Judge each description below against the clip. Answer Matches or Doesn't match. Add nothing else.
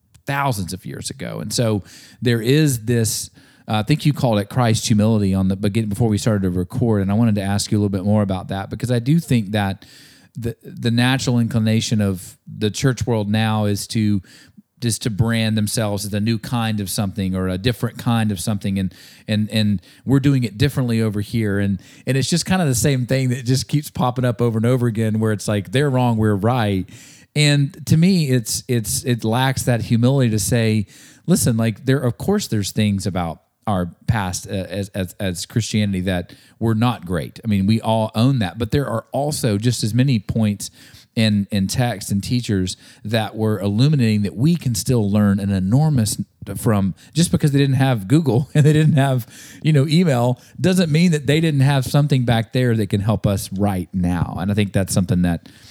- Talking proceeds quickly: Matches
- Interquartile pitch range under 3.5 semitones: Doesn't match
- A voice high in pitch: Doesn't match